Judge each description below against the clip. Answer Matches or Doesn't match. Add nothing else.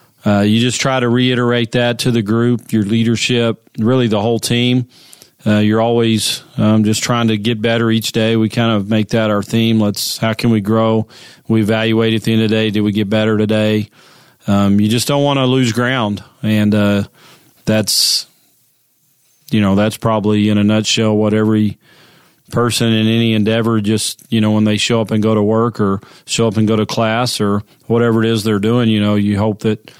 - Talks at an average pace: Doesn't match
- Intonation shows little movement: Matches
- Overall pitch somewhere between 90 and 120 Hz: Matches